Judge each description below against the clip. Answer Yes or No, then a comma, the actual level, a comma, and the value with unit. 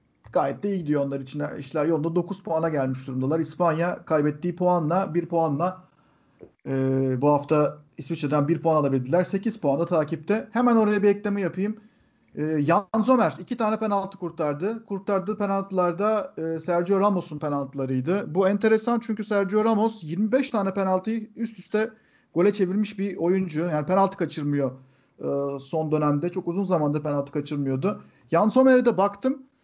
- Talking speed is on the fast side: Yes, fast, 145 wpm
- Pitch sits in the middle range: Yes, medium, 175 Hz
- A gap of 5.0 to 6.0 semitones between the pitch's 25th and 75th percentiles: Yes, wide, 5.4 semitones